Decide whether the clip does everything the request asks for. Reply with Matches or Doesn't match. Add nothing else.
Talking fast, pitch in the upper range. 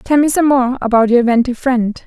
Matches